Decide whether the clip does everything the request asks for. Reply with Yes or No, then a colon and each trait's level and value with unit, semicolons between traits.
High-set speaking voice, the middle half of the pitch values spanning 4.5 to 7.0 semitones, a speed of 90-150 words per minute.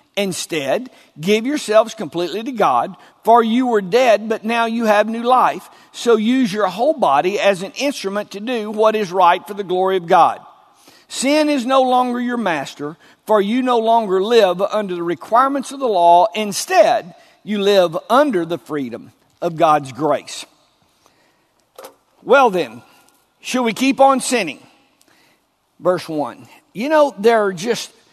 No: high, 220 Hz; average, 5.0 semitones; average, 160 wpm